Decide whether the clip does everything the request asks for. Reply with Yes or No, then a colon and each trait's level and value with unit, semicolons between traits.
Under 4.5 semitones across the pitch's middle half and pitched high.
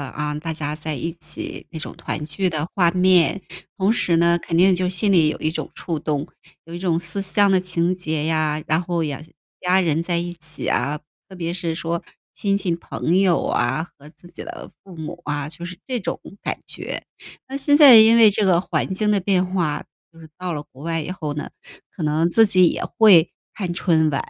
No: average, 3.0 semitones; medium, 170 Hz